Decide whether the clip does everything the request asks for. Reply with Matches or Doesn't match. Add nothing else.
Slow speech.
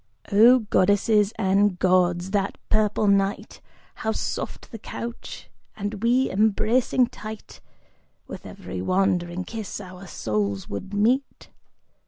Matches